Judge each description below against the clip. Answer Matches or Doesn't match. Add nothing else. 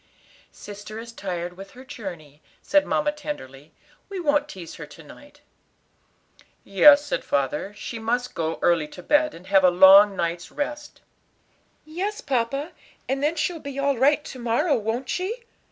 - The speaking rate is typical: Matches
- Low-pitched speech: Doesn't match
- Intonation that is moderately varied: Doesn't match